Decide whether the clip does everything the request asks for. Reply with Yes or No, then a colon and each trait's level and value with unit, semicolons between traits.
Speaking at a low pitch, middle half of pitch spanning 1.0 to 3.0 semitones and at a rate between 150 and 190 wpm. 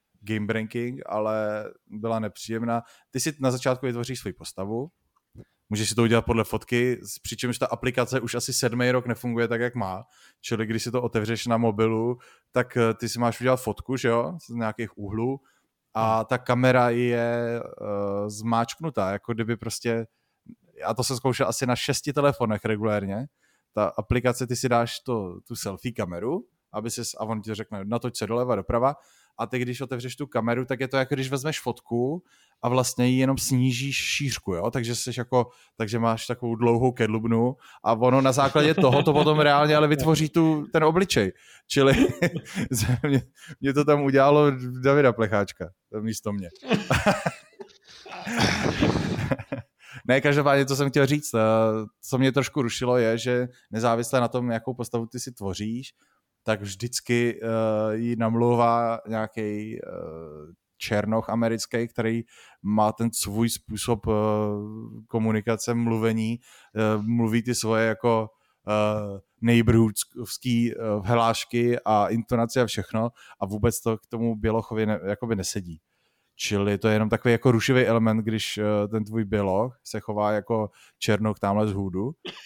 Yes: low, 115 Hz; narrow, 2.5 semitones; average, 155 wpm